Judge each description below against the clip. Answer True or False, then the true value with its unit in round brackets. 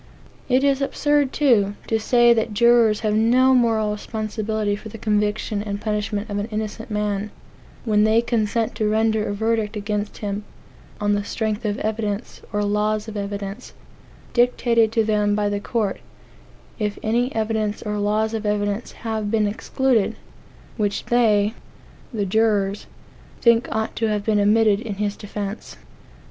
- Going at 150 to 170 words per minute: True (155 wpm)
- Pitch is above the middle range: True (215 Hz)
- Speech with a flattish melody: True (1.5 semitones)